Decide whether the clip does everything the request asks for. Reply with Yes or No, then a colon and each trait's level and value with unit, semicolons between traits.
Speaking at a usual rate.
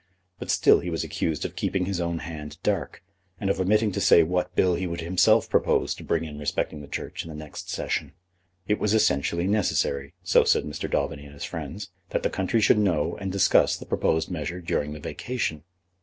No: fast, 210 wpm